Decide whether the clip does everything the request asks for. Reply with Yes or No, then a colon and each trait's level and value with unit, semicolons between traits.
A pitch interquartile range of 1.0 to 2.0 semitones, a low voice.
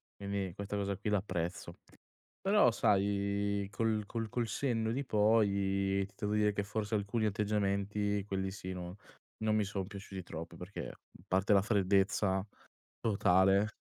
Yes: narrow, 1.6 semitones; low, 100 Hz